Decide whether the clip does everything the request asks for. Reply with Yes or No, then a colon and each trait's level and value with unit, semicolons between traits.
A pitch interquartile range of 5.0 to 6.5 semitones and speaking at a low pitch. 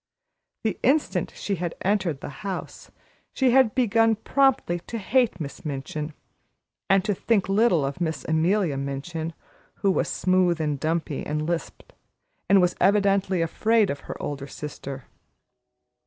No: wide, 5.5 semitones; medium, 180 Hz